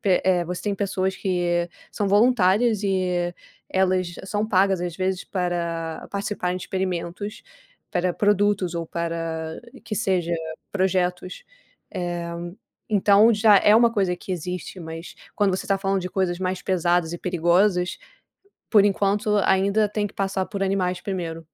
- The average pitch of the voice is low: No, medium, 185 Hz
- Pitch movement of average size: No, narrow, 2.3 semitones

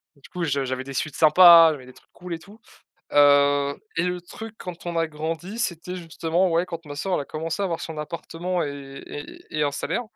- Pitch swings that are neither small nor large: Yes, average, 3.7 semitones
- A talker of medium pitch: Yes, medium, 165 Hz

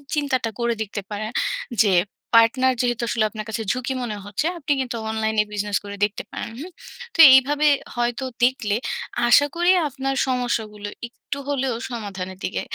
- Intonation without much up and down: No, average, 3.7 semitones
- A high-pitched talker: Yes, high, 235 Hz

